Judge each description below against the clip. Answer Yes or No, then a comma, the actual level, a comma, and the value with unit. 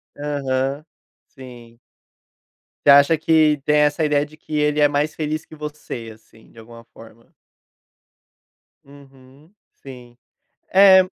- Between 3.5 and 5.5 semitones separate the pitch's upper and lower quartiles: No, average, 2.8 semitones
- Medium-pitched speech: Yes, medium, 145 Hz